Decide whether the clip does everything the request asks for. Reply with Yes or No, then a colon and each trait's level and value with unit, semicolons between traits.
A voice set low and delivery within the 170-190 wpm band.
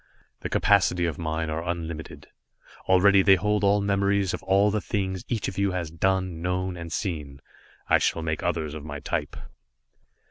Yes: very low, 90 Hz; average, 175 wpm